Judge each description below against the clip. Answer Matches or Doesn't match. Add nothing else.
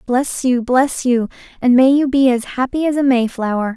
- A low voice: Doesn't match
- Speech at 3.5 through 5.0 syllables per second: Matches